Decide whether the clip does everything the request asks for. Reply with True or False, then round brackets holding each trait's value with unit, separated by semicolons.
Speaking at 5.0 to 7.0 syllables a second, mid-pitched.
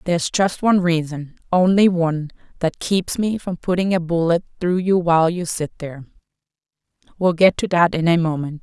True (5.4 syllables/s; 175 Hz)